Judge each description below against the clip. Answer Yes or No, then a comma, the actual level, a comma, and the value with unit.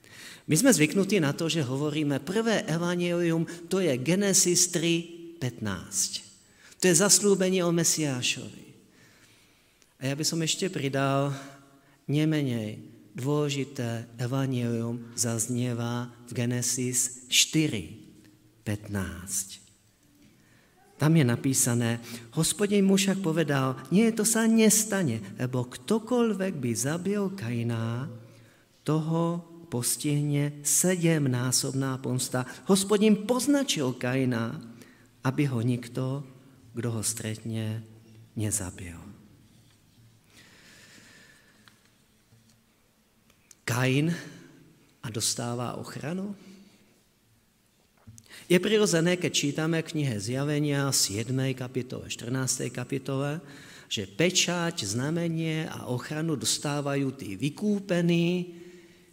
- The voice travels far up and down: Yes, wide, 6.1 semitones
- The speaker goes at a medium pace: No, slow, 85 wpm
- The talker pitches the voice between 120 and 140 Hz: Yes, low, 135 Hz